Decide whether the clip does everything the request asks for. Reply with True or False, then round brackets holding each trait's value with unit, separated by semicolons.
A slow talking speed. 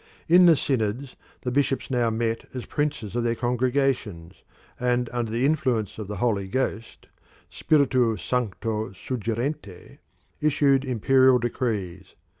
True (125 wpm)